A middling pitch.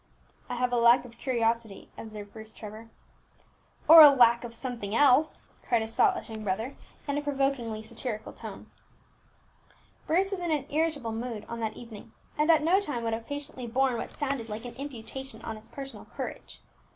No: high, 240 Hz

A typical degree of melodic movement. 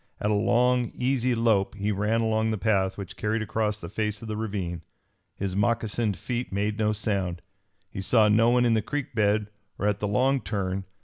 No: narrow, 2.2 semitones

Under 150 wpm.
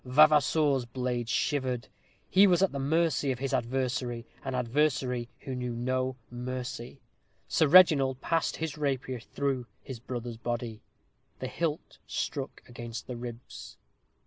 Yes: slow, 135 wpm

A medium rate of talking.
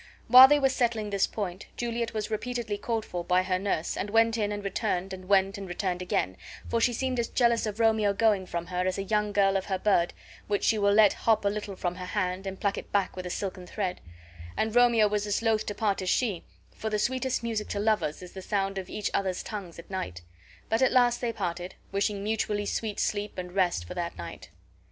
No: fast, 235 wpm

